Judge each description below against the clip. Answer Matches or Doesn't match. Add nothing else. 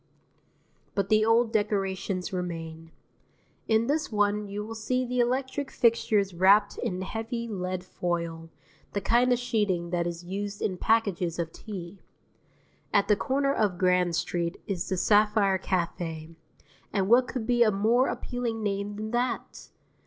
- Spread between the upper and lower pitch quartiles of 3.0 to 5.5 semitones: Matches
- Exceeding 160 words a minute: Doesn't match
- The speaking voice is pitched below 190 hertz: Doesn't match